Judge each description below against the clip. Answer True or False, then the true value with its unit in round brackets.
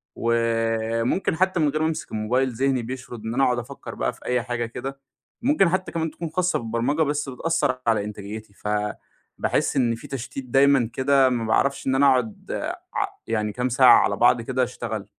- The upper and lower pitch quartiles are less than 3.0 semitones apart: False (3.3 semitones)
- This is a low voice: True (125 Hz)